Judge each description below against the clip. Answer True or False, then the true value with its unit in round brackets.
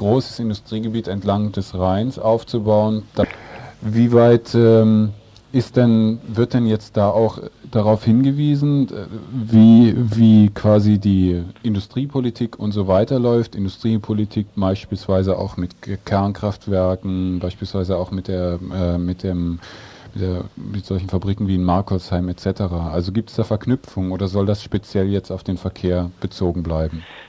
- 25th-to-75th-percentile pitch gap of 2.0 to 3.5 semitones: True (3.1 semitones)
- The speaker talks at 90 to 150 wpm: True (140 wpm)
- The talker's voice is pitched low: True (105 Hz)